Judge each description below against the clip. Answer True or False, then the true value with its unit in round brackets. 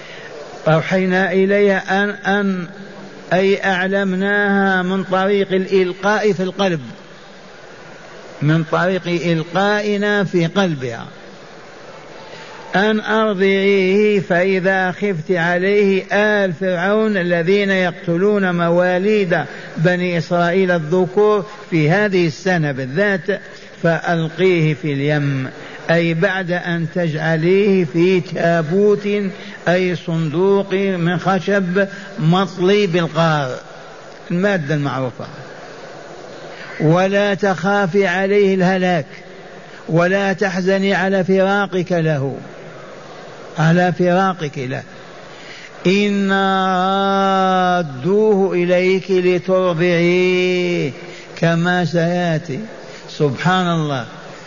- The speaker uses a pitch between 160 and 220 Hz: True (185 Hz)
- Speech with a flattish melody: True (2.2 semitones)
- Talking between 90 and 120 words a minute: False (75 wpm)